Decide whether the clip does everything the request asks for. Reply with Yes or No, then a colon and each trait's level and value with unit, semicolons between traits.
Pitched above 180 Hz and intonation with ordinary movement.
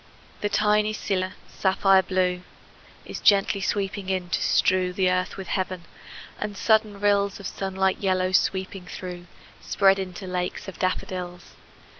No: high, 190 Hz; narrow, 1.4 semitones